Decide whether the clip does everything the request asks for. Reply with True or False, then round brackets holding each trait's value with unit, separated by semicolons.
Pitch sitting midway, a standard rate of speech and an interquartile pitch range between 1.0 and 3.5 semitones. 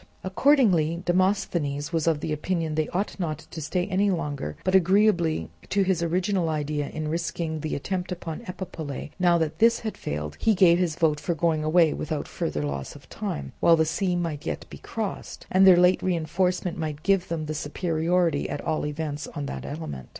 True (165 Hz; 190 wpm; 3.2 semitones)